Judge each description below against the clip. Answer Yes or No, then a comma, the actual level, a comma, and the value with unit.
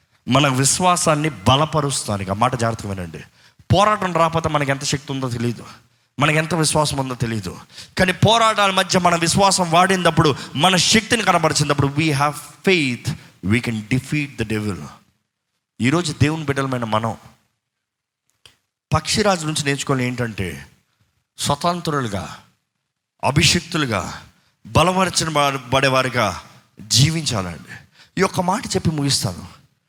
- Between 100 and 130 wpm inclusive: Yes, average, 105 wpm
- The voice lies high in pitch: No, medium, 140 Hz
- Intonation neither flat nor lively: No, wide, 5.9 semitones